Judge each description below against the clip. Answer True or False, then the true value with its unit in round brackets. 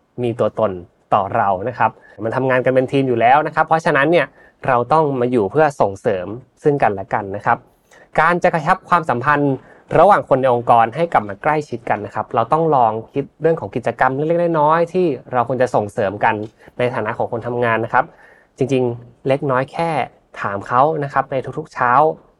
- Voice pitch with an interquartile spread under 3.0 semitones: False (4.5 semitones)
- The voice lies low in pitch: True (130 Hz)